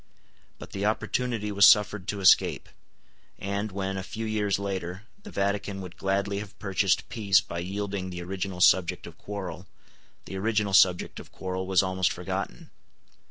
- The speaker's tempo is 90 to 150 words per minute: No, average, 160 wpm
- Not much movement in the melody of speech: Yes, narrow, 1.6 semitones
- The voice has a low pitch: Yes, low, 100 Hz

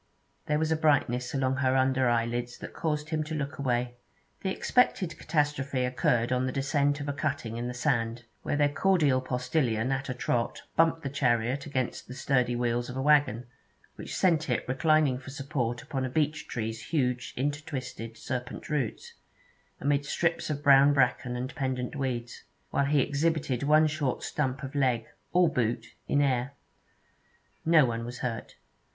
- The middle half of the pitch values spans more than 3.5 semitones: No, average, 3.1 semitones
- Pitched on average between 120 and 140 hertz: Yes, low, 135 Hz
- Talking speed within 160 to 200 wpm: Yes, average, 170 wpm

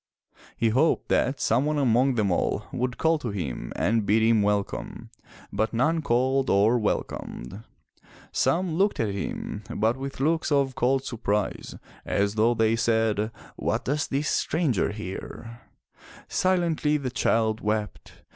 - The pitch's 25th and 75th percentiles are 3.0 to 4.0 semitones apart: No, average, 4.4 semitones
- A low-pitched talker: Yes, low, 115 Hz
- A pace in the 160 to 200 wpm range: No, average, 145 wpm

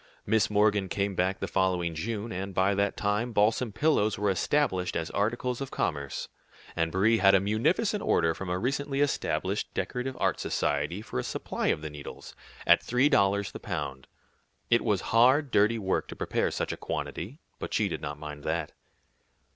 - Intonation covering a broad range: No, average, 4.4 semitones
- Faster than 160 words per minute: Yes, average, 180 wpm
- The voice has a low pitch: Yes, low, 100 Hz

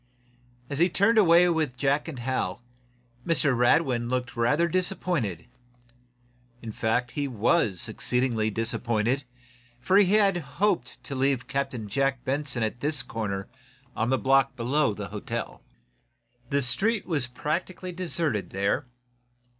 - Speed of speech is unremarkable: No, slow, 130 wpm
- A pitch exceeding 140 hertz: No, low, 135 Hz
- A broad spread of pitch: Yes, wide, 5.7 semitones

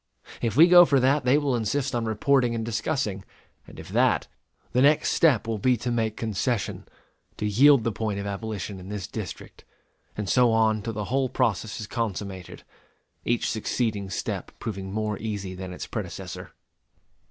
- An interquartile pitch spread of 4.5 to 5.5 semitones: No, average, 3.5 semitones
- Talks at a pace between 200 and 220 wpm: No, average, 175 wpm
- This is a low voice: Yes, low, 110 Hz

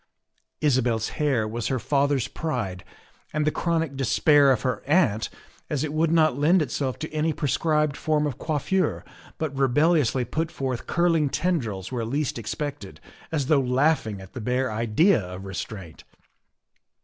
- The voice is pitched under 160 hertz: Yes, medium, 140 Hz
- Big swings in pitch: No, average, 4.7 semitones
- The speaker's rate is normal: Yes, average, 155 wpm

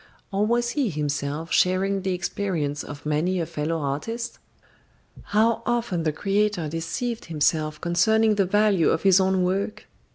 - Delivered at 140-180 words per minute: Yes, average, 150 wpm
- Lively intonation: No, average, 4.9 semitones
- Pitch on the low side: No, medium, 185 Hz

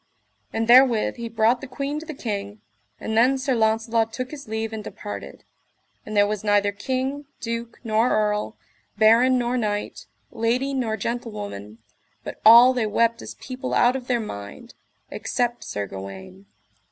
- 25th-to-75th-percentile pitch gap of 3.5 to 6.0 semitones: No, average, 3.0 semitones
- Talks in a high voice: Yes, high, 230 Hz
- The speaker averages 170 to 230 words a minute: No, average, 160 wpm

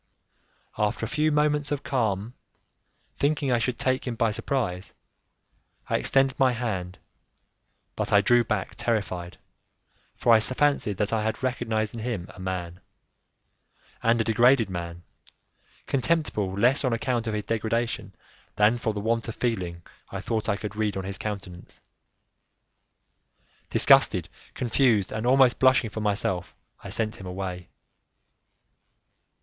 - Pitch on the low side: Yes, low, 110 Hz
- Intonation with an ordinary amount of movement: Yes, average, 4.0 semitones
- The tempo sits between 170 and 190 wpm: No, average, 140 wpm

